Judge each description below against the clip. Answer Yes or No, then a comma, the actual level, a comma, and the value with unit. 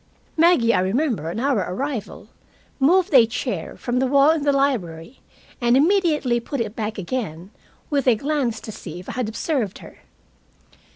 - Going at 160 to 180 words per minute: Yes, average, 170 wpm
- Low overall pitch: No, very high, 250 Hz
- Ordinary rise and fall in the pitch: Yes, average, 5.0 semitones